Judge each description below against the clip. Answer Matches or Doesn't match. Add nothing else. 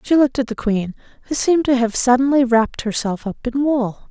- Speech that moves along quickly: Matches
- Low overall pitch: Doesn't match